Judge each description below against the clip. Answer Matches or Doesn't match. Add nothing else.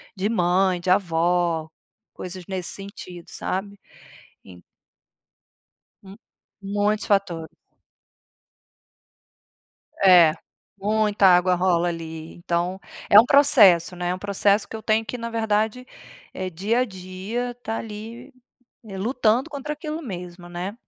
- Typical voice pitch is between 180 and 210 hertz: Matches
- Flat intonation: Doesn't match